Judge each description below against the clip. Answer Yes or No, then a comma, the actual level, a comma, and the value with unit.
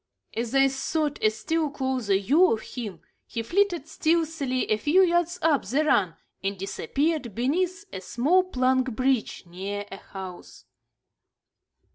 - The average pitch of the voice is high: Yes, very high, 265 Hz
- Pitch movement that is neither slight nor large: No, wide, 7.0 semitones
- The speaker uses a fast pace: No, average, 140 wpm